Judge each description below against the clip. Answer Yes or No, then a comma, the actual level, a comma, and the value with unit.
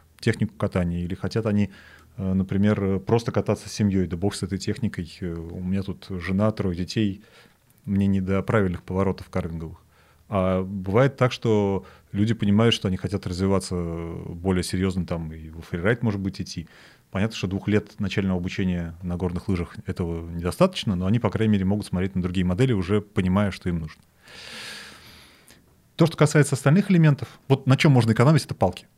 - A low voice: Yes, very low, 95 Hz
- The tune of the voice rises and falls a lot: No, average, 3.0 semitones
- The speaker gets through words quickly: Yes, fast, 175 wpm